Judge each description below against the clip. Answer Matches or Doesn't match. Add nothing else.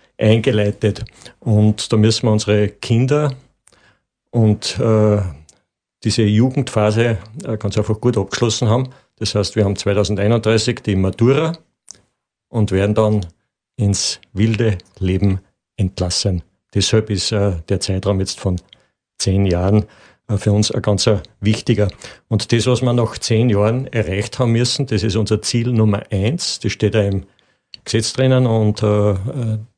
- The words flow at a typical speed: Matches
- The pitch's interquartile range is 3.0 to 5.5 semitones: Doesn't match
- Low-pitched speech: Matches